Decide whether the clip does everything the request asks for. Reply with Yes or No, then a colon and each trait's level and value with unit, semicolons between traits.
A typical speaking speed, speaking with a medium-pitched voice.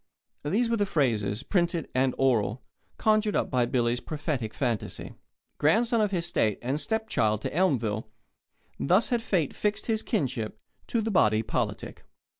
Yes: average, 150 wpm; medium, 145 Hz